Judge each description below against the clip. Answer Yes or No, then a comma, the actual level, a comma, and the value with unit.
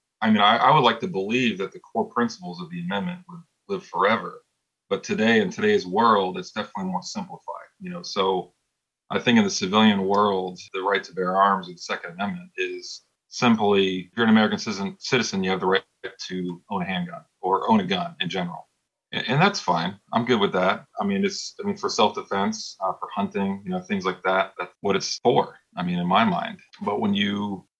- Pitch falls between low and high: Yes, medium, 180 Hz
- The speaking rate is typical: No, fast, 220 wpm